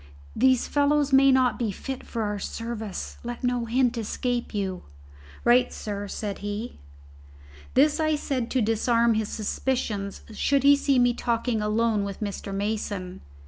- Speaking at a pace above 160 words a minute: No, average, 150 wpm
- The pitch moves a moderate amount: Yes, average, 3.8 semitones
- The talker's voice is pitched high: Yes, high, 235 Hz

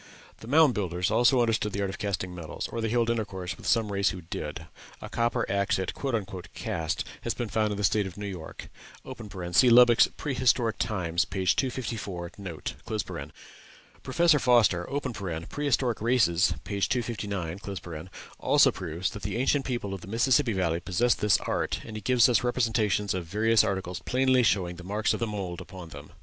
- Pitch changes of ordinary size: Yes, average, 4.3 semitones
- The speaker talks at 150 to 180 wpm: Yes, average, 175 wpm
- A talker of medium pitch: No, low, 105 Hz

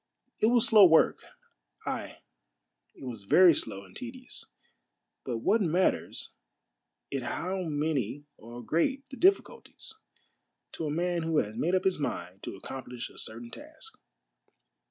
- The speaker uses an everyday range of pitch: No, wide, 7.8 semitones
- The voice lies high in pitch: No, medium, 160 Hz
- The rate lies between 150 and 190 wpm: No, average, 140 wpm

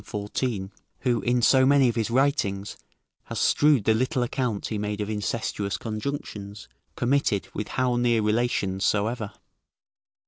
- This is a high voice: No, low, 115 Hz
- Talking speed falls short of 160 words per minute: Yes, average, 140 wpm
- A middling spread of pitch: Yes, average, 3.6 semitones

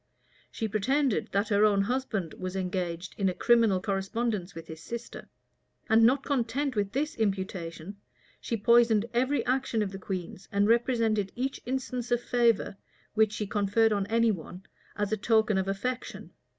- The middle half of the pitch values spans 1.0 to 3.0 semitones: No, average, 3.6 semitones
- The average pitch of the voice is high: Yes, high, 215 Hz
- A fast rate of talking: No, average, 165 wpm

